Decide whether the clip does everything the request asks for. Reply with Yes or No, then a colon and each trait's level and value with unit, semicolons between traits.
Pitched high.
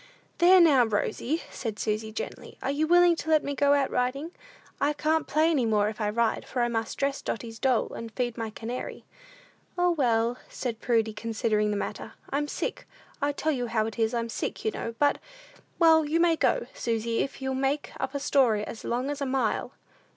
Yes: very high, 250 Hz